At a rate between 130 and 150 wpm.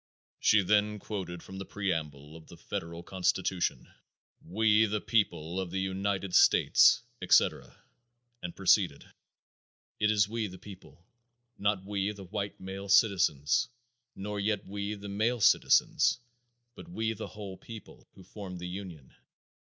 Yes: average, 140 wpm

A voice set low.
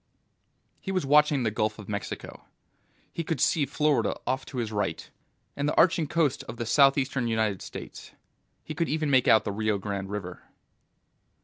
Yes: low, 130 Hz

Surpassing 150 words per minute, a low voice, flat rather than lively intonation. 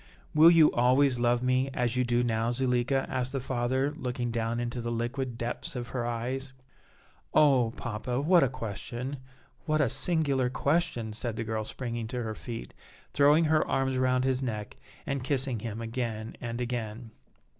Yes: average, 170 wpm; low, 125 Hz; narrow, 2.3 semitones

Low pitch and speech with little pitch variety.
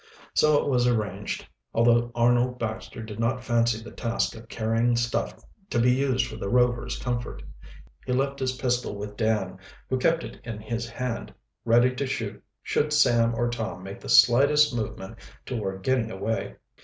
Yes: low, 120 Hz; narrow, 2.0 semitones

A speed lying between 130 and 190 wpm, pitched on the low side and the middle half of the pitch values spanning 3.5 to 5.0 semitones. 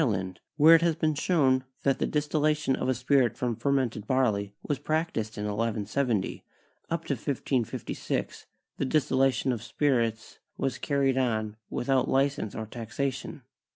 Yes: average, 150 wpm; low, 130 Hz; average, 4.1 semitones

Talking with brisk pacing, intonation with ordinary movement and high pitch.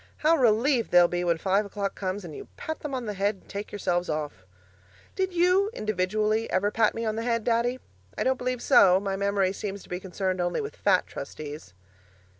Yes: fast, 210 wpm; average, 4.2 semitones; high, 205 Hz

